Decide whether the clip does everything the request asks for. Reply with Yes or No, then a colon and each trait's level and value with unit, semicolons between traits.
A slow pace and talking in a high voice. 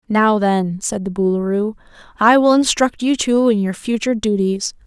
No: average, 175 wpm; high, 215 Hz